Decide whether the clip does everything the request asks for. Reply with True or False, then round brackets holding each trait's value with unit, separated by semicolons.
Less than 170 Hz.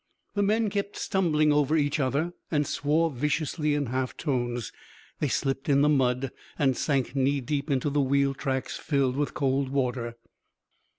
True (140 Hz)